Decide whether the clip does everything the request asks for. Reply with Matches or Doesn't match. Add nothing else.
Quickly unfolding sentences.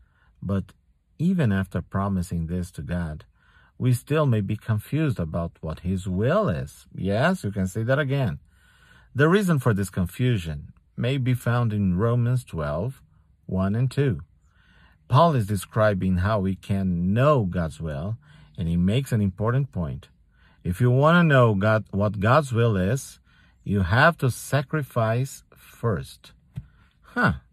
Doesn't match